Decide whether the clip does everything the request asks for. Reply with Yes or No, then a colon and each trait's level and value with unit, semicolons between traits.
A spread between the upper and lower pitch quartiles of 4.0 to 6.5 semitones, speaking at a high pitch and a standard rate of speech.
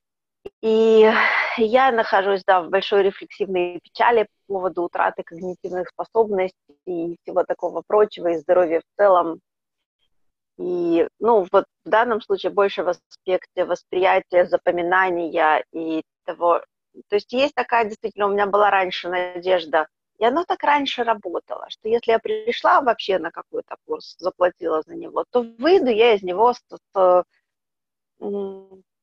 Yes: average, 4.3 semitones; high, 195 Hz; average, 135 wpm